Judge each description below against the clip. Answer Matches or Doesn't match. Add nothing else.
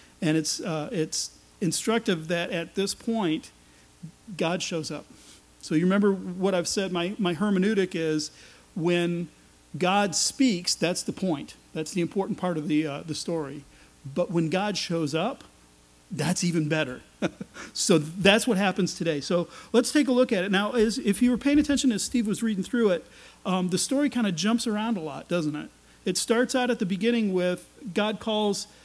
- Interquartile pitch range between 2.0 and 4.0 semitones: Doesn't match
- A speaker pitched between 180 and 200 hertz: Matches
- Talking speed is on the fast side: Doesn't match